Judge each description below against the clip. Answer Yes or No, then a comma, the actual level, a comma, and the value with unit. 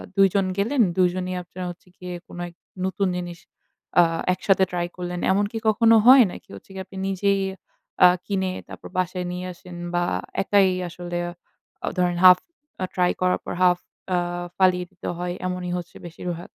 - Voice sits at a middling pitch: Yes, medium, 180 Hz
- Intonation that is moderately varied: No, narrow, 1.5 semitones